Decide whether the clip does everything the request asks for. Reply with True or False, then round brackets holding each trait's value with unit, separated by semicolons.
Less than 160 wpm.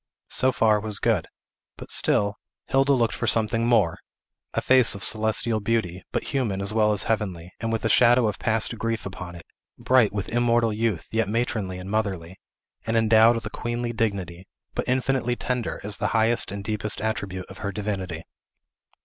False (180 wpm)